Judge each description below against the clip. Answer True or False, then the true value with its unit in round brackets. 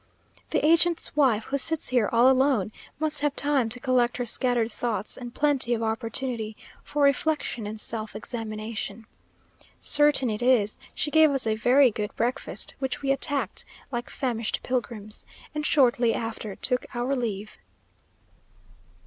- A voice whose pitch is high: True (245 Hz)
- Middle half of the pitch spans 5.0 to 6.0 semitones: False (3.7 semitones)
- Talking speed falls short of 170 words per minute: True (150 wpm)